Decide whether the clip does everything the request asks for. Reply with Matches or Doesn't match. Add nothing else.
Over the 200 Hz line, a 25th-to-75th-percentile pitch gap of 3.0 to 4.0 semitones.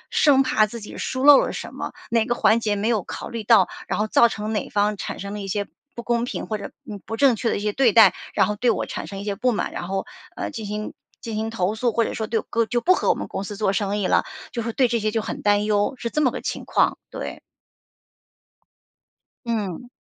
Doesn't match